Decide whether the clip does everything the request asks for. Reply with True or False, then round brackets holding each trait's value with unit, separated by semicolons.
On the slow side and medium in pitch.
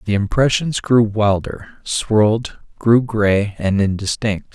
False (120 wpm; 110 Hz)